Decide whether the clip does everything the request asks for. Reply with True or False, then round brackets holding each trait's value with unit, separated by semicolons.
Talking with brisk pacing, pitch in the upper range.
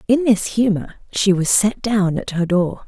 True (210 wpm; 200 Hz)